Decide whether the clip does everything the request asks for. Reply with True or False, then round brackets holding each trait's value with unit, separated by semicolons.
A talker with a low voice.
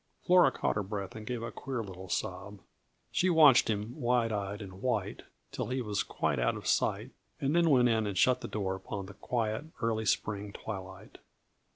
True (110 Hz)